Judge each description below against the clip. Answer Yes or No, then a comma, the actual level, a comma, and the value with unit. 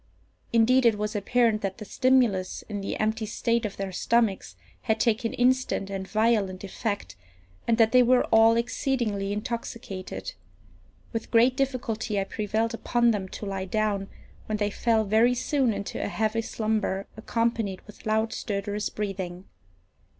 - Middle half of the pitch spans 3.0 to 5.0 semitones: No, narrow, 2.6 semitones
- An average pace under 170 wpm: Yes, average, 150 wpm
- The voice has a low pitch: No, high, 220 Hz